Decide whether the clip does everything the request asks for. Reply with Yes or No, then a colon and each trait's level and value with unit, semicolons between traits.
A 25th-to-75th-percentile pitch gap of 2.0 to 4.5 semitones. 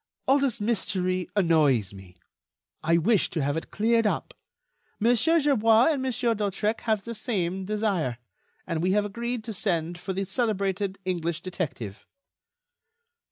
No: average, 4.9 semitones